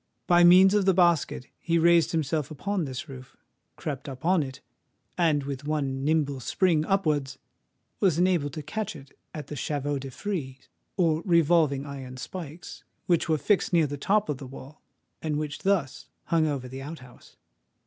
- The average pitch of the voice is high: No, medium, 155 Hz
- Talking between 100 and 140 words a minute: No, average, 165 wpm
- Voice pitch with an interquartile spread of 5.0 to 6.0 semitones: No, average, 3.9 semitones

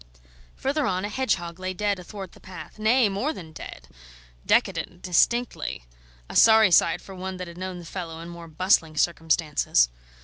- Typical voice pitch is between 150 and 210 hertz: Yes, medium, 185 Hz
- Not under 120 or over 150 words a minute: No, average, 170 wpm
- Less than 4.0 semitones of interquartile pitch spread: Yes, average, 3.5 semitones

